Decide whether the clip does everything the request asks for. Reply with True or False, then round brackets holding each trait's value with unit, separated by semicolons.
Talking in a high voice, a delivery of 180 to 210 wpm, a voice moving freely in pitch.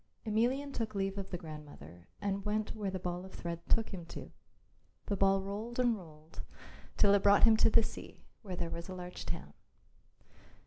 False (195 Hz; 190 wpm; 3.7 semitones)